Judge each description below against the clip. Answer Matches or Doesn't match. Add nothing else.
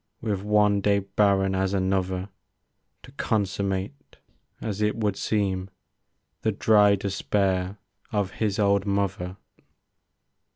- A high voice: Doesn't match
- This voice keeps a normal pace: Doesn't match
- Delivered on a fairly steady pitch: Matches